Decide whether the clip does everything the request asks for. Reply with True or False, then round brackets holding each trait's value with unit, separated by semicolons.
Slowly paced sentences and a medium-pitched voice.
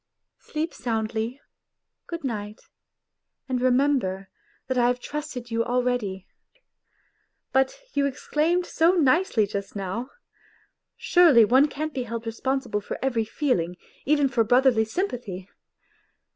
False (125 wpm; 250 Hz)